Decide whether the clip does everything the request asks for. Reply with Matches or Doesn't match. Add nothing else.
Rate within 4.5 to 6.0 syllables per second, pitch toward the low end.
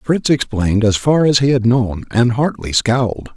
Matches